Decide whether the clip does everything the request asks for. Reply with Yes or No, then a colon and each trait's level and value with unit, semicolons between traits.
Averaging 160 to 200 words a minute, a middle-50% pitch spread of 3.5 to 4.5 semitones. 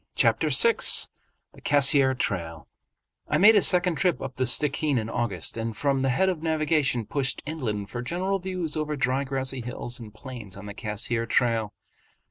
No: average, 175 wpm; average, 5.1 semitones